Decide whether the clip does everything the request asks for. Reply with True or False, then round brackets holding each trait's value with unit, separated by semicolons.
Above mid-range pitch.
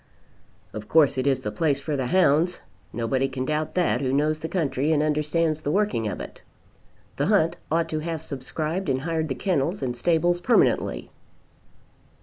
False (150 Hz)